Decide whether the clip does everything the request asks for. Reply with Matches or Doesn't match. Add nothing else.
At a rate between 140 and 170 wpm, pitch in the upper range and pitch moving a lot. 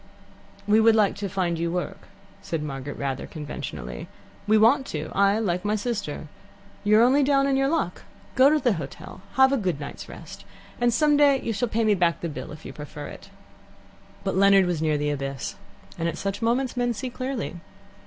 Doesn't match